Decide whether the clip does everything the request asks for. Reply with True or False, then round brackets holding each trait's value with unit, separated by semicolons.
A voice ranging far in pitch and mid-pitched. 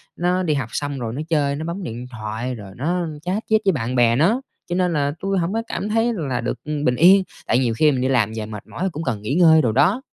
True (6.5 semitones; 145 Hz)